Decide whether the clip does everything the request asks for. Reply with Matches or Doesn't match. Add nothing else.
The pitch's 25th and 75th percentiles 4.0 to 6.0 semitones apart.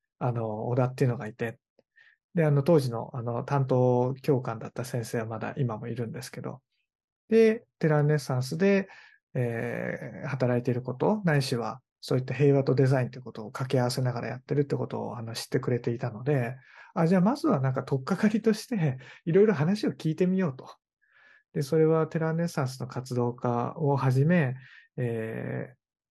Matches